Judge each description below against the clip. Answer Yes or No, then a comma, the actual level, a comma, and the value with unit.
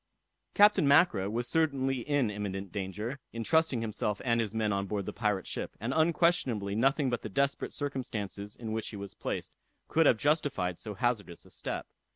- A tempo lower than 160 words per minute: No, average, 185 wpm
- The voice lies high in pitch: No, low, 115 Hz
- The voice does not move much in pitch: No, wide, 5.4 semitones